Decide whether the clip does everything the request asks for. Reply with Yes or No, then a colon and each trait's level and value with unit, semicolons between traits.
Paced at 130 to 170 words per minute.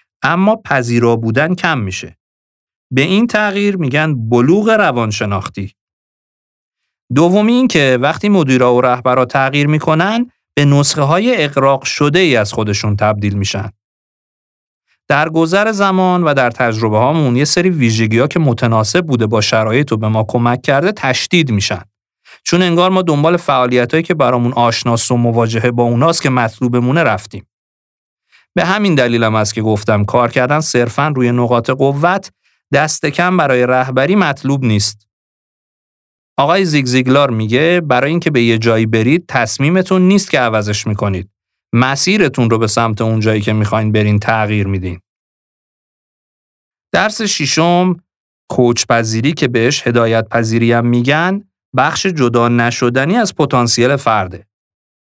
Yes: average, 135 wpm